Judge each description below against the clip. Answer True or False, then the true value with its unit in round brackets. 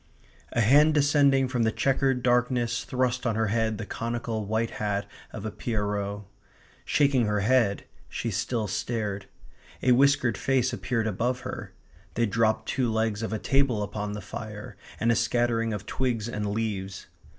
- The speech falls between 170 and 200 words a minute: False (160 wpm)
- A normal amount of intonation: True (3.1 semitones)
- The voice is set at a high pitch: False (115 Hz)